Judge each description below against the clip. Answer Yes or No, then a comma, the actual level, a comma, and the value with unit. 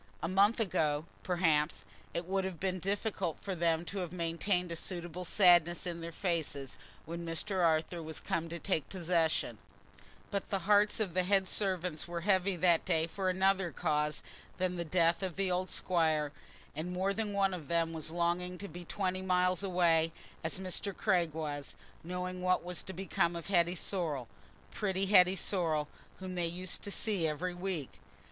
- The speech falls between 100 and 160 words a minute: No, average, 175 wpm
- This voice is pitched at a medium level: Yes, medium, 180 Hz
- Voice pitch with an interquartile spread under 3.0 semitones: Yes, narrow, 2.4 semitones